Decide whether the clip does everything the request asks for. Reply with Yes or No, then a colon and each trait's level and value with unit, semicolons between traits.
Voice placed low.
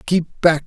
No: medium, 165 Hz